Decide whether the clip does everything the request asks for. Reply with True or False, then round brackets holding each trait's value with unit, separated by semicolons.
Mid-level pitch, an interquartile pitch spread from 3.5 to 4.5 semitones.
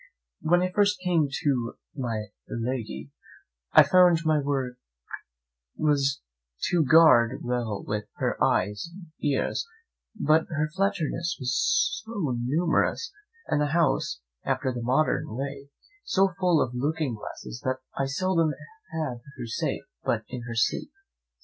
False (145 Hz; 5.2 semitones)